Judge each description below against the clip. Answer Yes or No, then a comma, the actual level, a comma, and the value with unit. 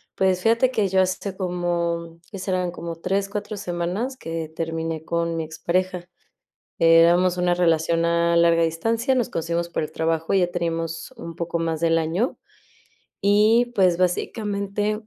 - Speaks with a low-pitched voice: No, medium, 175 Hz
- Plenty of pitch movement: No, average, 2.8 semitones